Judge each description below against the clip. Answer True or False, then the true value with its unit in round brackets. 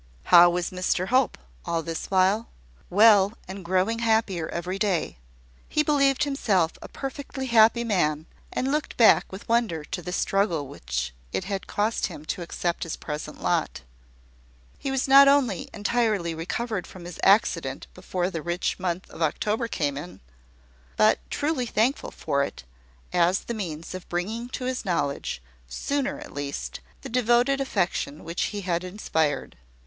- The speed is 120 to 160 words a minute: True (155 wpm)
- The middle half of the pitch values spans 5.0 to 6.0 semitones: True (5.6 semitones)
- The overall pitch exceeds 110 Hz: True (190 Hz)